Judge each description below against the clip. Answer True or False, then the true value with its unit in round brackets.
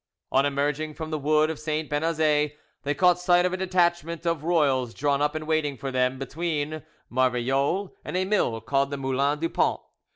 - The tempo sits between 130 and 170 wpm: False (190 wpm)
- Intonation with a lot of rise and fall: False (3.1 semitones)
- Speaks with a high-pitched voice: False (150 Hz)